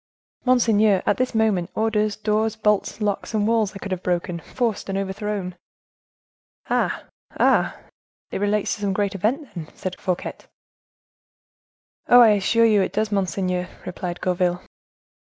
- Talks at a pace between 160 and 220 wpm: No, average, 145 wpm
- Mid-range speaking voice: No, high, 205 Hz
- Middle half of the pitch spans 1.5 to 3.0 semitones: Yes, average, 2.7 semitones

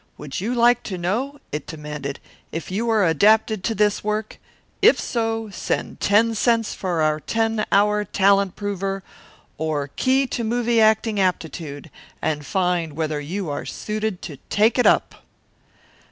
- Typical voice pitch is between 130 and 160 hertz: No, high, 200 Hz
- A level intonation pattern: No, wide, 5.4 semitones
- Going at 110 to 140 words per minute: No, average, 155 wpm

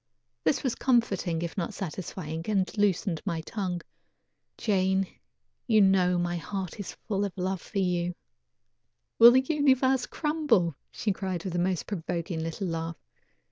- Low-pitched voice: No, high, 190 Hz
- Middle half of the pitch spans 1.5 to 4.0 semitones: Yes, average, 3.3 semitones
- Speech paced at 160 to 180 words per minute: No, average, 150 wpm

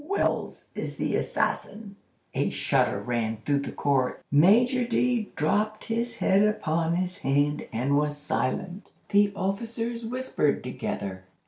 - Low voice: No, high, 190 Hz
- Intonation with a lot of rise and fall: Yes, wide, 7.8 semitones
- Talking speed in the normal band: No, slow, 130 wpm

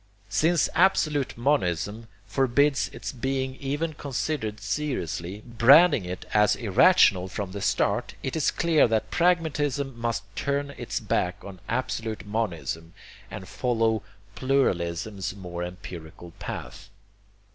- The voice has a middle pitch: No, low, 115 Hz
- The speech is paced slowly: Yes, slow, 115 wpm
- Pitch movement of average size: No, wide, 6.5 semitones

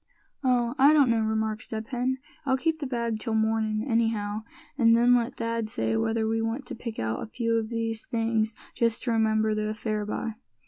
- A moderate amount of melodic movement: No, narrow, 1.5 semitones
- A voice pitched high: Yes, high, 225 Hz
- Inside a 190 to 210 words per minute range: Yes, average, 200 wpm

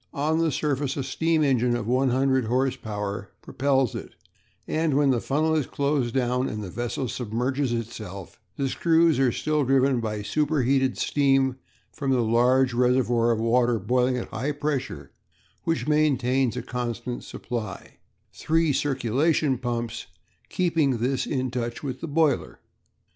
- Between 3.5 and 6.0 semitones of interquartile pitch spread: No, average, 3.1 semitones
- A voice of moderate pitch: No, low, 130 Hz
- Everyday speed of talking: Yes, average, 150 wpm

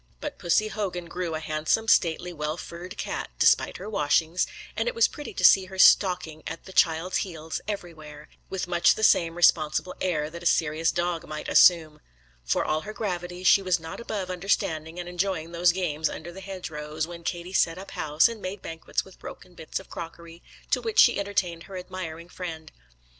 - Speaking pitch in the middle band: Yes, medium, 175 Hz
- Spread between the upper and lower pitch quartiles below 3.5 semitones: Yes, average, 2.7 semitones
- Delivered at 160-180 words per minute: No, average, 190 wpm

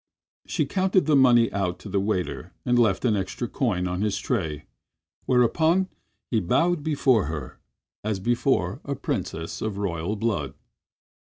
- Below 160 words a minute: Yes, average, 150 wpm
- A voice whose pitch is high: No, low, 110 Hz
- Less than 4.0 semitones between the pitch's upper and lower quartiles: No, wide, 5.6 semitones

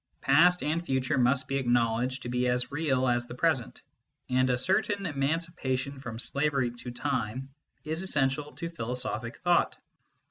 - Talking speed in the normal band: Yes, average, 150 wpm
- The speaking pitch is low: Yes, low, 130 Hz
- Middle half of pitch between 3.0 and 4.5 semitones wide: Yes, average, 3.7 semitones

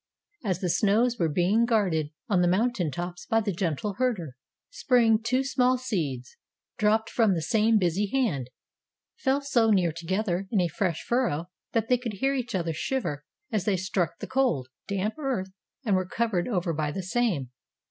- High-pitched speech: Yes, high, 200 Hz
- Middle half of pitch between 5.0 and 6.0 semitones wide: Yes, average, 5.3 semitones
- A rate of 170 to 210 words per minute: Yes, average, 180 wpm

